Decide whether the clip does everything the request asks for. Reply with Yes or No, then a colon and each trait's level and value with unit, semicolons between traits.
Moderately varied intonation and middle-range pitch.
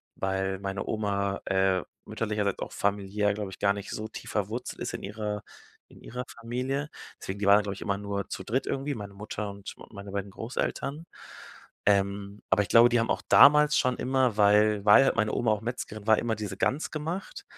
No: average, 3.0 semitones; low, 105 Hz